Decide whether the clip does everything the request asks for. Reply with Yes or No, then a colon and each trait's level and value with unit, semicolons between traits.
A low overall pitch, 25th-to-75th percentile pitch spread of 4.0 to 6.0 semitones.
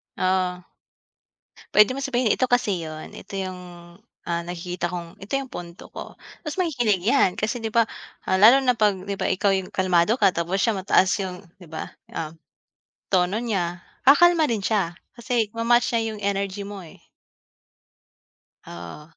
No: high, 195 Hz; average, 4.5 semitones